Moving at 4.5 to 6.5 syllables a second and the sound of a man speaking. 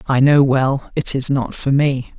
No: 4.0 syllables/s; male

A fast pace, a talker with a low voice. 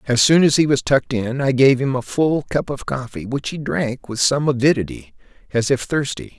Yes: fast, 225 wpm; low, 130 Hz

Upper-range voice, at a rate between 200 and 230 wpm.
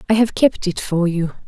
No: high, 195 Hz; fast, 245 wpm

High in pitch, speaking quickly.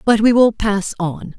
Yes: high, 210 Hz; fast, 215 wpm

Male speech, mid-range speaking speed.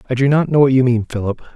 No: male; fast, 310 wpm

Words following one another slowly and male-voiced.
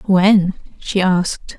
No: slow, 115 wpm; female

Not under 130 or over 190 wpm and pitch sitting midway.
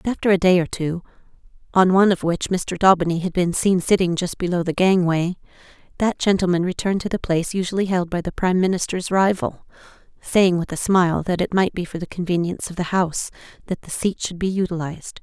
No: average, 200 wpm; medium, 180 Hz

